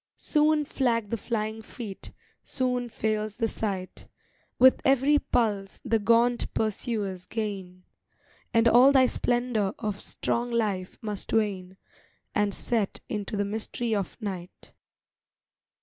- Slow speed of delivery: Yes, slow, 120 wpm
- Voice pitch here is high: Yes, high, 220 Hz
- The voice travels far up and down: No, average, 3.1 semitones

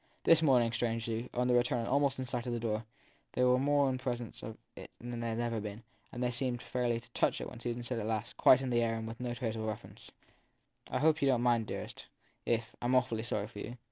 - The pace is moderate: No, fast, 260 wpm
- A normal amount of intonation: No, narrow, 1.8 semitones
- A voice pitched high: No, low, 120 Hz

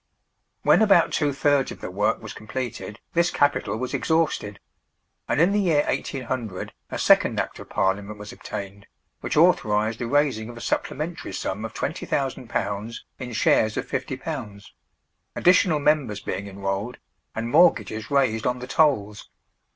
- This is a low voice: Yes, low, 120 Hz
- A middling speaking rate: Yes, average, 150 wpm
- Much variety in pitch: Yes, wide, 5.8 semitones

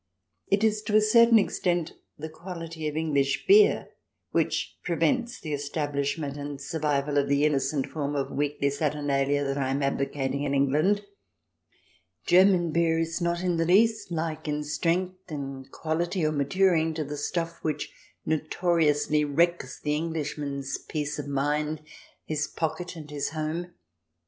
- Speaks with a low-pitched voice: No, medium, 155 Hz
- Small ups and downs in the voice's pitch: No, average, 3.2 semitones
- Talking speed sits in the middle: Yes, average, 155 wpm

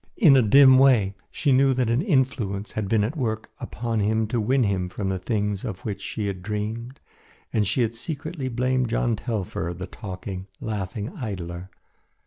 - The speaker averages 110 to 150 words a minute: No, average, 180 wpm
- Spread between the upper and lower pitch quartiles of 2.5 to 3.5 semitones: No, average, 4.4 semitones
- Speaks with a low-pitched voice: Yes, low, 110 Hz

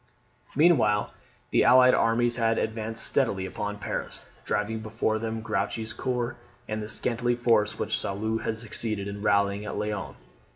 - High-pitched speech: No, low, 110 Hz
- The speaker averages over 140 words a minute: Yes, average, 150 wpm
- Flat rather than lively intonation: Yes, narrow, 2.0 semitones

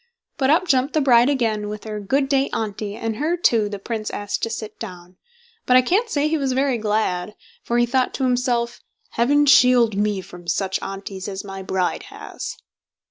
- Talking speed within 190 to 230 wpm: Yes, average, 195 wpm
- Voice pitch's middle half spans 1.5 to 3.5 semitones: No, average, 4.5 semitones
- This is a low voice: No, high, 230 Hz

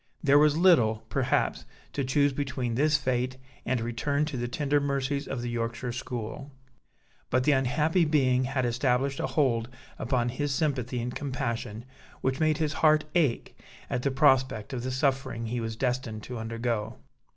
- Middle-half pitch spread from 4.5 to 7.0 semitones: No, average, 3.0 semitones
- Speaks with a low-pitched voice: Yes, low, 130 Hz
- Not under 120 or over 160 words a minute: No, average, 170 wpm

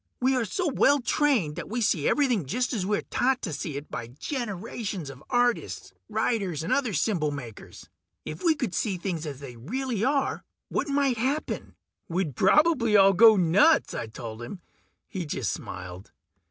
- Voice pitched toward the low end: No, high, 205 Hz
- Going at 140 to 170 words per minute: No, average, 180 wpm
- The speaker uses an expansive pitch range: Yes, wide, 8.9 semitones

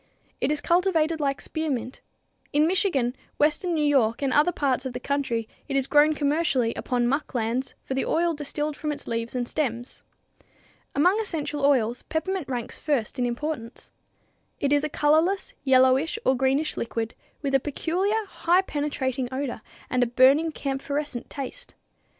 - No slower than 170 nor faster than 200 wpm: No, average, 160 wpm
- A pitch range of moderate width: Yes, average, 3.4 semitones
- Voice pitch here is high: Yes, very high, 285 Hz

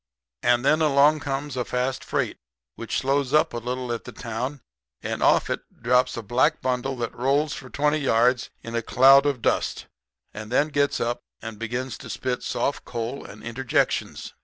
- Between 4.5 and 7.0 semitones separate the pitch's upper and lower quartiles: No, average, 2.8 semitones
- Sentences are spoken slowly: No, average, 185 wpm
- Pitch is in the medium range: No, low, 130 Hz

